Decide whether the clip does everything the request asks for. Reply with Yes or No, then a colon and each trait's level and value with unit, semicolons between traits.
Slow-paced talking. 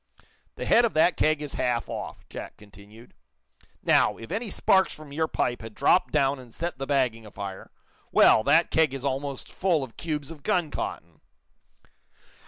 No: average, 175 wpm